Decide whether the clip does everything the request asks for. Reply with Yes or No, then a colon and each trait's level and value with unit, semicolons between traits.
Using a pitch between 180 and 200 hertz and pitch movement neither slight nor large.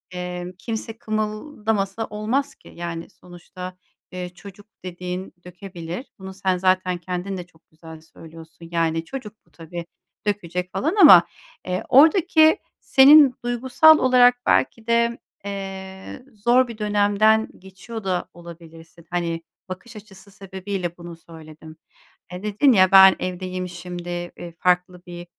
Yes: medium, 185 Hz; average, 3.7 semitones